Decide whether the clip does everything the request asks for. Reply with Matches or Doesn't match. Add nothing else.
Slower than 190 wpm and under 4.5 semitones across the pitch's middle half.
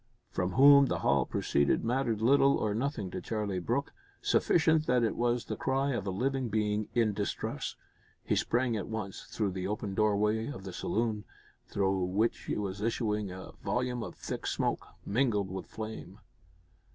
Matches